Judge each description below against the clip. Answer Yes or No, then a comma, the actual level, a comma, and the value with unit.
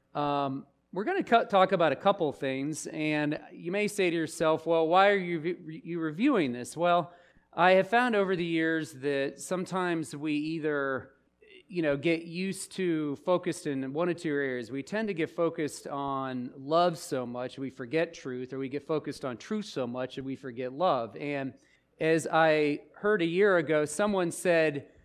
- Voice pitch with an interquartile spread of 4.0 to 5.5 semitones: Yes, average, 4.3 semitones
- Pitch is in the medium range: Yes, medium, 160 Hz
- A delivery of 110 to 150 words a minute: No, average, 185 wpm